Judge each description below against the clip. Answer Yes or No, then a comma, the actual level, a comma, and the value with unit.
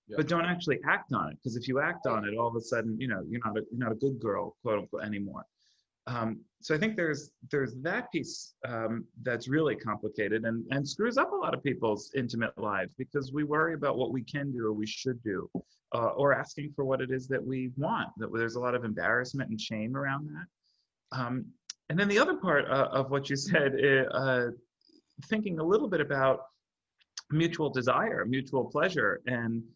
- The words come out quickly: Yes, fast, 210 wpm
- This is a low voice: Yes, low, 130 Hz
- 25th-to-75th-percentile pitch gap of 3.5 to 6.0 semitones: Yes, average, 4.3 semitones